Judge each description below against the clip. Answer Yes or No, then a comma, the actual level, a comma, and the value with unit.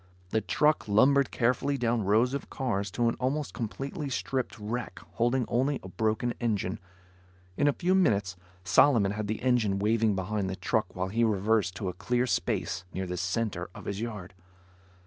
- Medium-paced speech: Yes, average, 175 wpm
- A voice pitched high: No, low, 110 Hz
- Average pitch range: Yes, average, 4.1 semitones